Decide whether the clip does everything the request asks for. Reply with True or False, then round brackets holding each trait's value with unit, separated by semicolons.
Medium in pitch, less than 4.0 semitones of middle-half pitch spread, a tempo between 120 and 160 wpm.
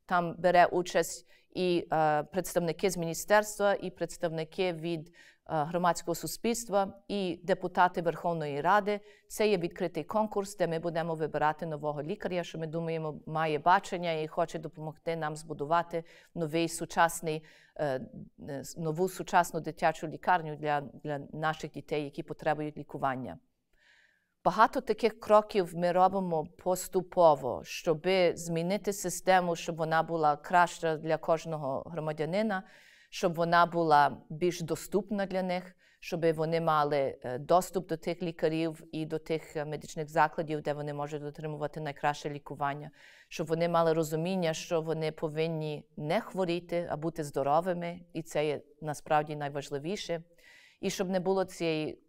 True (165 Hz; 2.7 semitones; 130 wpm)